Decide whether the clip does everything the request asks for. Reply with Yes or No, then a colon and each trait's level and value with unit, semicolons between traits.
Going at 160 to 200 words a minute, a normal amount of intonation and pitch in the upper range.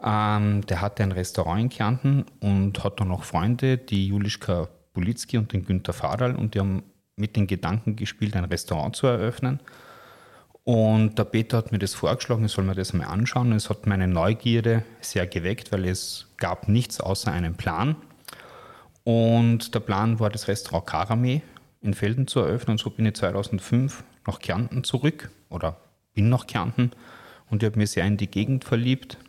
No: average, 180 wpm; average, 3.3 semitones; low, 110 Hz